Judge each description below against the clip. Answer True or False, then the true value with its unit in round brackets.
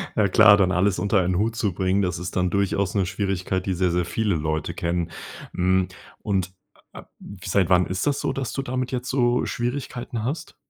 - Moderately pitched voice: False (95 Hz)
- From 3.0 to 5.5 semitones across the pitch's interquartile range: True (3.7 semitones)